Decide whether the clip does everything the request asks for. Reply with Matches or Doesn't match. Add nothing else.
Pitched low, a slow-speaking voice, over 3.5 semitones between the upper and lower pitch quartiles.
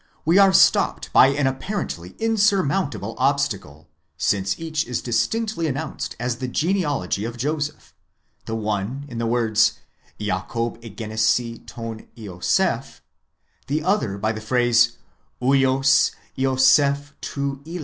Matches